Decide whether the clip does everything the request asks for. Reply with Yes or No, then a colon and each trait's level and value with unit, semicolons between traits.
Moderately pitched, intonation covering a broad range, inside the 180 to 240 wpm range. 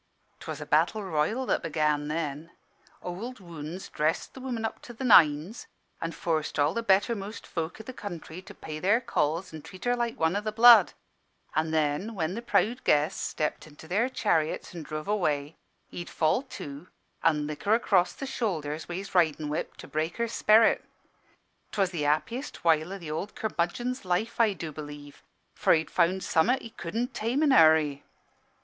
Yes: medium, 175 Hz; wide, 6.1 semitones; average, 185 wpm